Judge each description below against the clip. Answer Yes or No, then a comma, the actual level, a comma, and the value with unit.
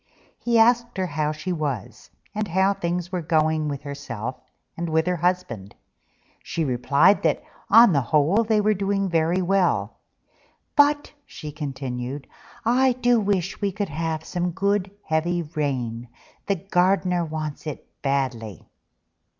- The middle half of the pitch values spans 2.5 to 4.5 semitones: No, wide, 5.4 semitones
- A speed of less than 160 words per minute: Yes, average, 140 wpm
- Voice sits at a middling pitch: Yes, medium, 170 Hz